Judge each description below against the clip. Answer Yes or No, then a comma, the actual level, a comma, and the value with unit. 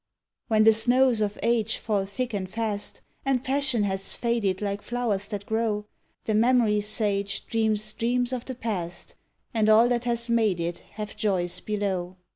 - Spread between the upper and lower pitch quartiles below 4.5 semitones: Yes, average, 2.7 semitones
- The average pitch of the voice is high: Yes, high, 215 Hz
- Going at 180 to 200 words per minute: No, average, 165 wpm